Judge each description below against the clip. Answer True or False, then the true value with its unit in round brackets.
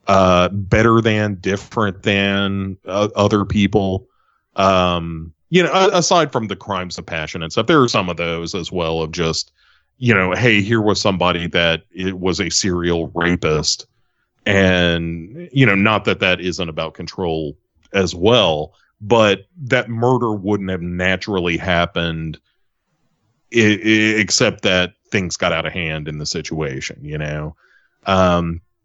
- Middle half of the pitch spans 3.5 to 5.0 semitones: True (3.8 semitones)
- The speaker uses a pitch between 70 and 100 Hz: True (95 Hz)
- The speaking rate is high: False (155 wpm)